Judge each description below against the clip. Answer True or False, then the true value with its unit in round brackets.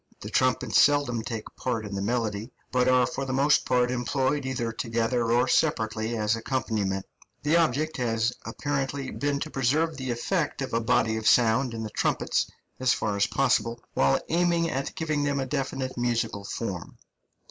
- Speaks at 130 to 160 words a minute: False (175 wpm)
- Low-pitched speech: True (125 Hz)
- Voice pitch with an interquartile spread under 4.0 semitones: True (3.4 semitones)